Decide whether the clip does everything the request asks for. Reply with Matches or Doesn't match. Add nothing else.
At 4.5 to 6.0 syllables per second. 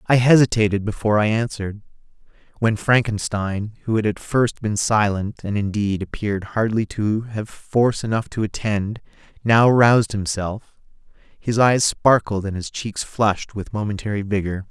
Matches